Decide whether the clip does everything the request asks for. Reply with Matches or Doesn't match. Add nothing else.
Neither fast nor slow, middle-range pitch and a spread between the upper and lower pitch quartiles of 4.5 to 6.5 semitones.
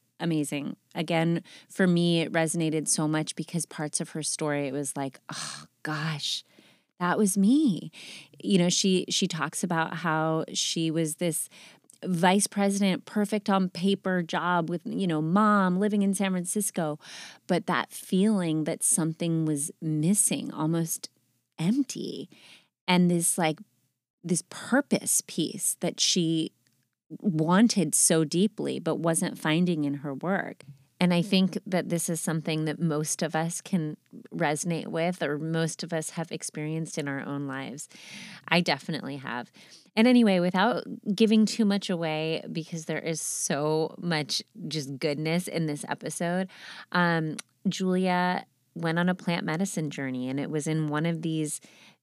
Doesn't match